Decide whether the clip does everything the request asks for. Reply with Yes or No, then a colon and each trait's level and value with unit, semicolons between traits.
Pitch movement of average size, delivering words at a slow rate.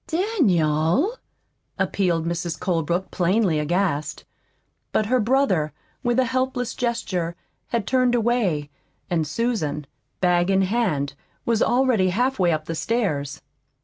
No: wide, 6.6 semitones; slow, 115 wpm